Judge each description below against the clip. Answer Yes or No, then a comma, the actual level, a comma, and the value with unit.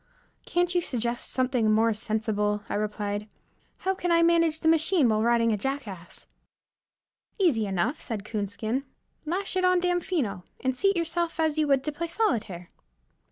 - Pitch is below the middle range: No, very high, 260 Hz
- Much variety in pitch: Yes, wide, 7.7 semitones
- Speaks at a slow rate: No, average, 160 wpm